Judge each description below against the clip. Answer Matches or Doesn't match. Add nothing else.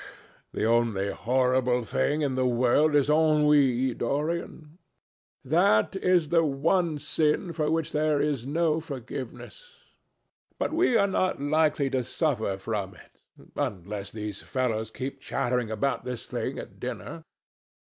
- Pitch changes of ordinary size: Matches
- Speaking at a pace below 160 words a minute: Matches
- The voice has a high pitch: Doesn't match